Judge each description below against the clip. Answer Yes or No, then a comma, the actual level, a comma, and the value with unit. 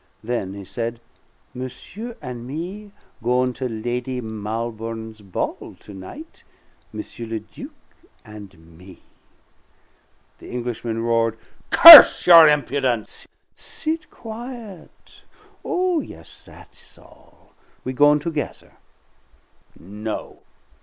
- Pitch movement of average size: No, wide, 7.0 semitones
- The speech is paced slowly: Yes, slow, 100 wpm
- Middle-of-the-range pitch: No, low, 125 Hz